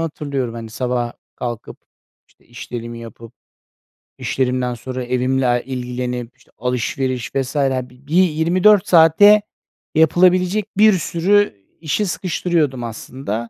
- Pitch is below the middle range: Yes, low, 130 Hz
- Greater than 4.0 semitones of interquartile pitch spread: Yes, wide, 5.4 semitones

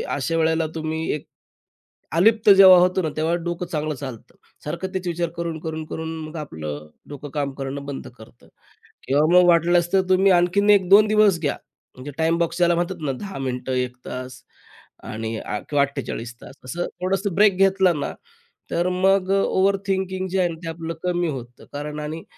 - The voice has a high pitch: No, medium, 165 Hz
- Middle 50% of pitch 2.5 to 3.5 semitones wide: No, average, 4.1 semitones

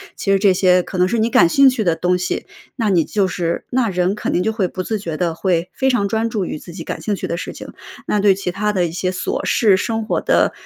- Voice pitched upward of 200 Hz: No, high, 190 Hz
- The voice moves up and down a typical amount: Yes, average, 3.3 semitones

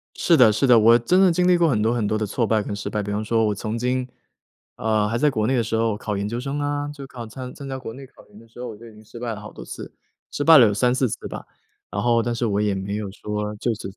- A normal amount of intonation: Yes, average, 3.3 semitones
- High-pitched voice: No, low, 115 Hz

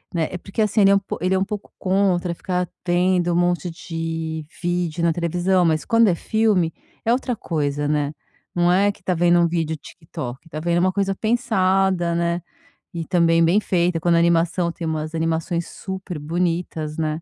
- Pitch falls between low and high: Yes, medium, 175 Hz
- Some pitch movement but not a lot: No, narrow, 2.3 semitones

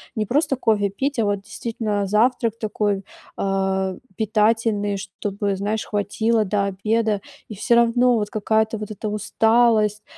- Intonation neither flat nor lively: No, narrow, 1.9 semitones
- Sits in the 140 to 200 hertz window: No, high, 215 Hz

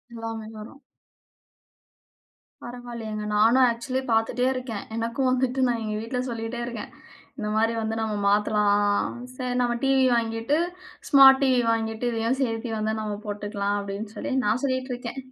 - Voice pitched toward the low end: No, high, 230 Hz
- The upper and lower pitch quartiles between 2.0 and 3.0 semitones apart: Yes, narrow, 2.6 semitones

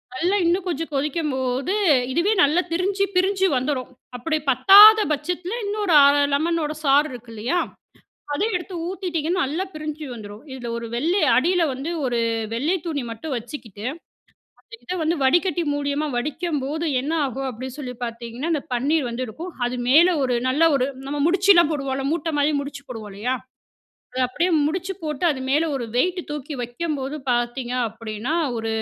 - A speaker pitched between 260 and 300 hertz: Yes, very high, 290 Hz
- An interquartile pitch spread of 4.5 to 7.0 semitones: Yes, average, 5.2 semitones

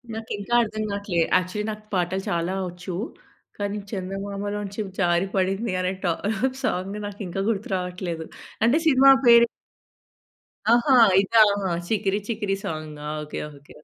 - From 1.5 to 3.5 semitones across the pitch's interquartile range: Yes, average, 2.9 semitones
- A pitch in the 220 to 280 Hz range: No, high, 195 Hz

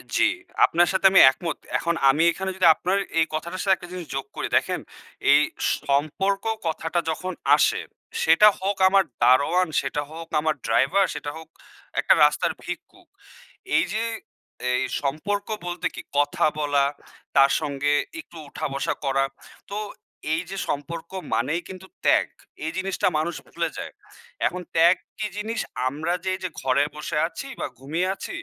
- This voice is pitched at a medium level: Yes, medium, 165 Hz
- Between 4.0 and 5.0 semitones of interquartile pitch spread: Yes, average, 4.5 semitones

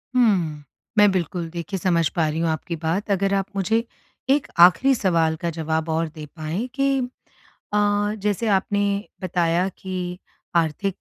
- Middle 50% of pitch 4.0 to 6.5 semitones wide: No, average, 3.6 semitones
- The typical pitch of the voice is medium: Yes, medium, 180 Hz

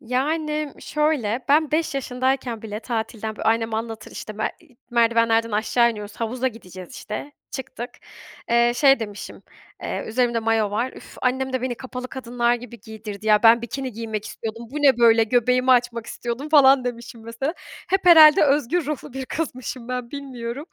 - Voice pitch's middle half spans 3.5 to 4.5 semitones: No, average, 3.0 semitones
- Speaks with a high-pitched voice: Yes, high, 240 Hz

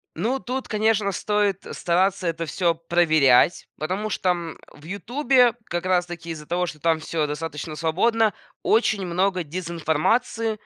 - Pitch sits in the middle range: Yes, medium, 175 Hz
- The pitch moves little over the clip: No, average, 4.3 semitones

